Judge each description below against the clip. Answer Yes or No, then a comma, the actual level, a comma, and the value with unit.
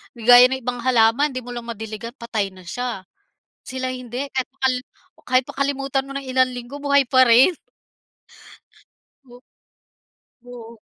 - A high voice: Yes, very high, 250 Hz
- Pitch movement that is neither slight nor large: No, narrow, 1.9 semitones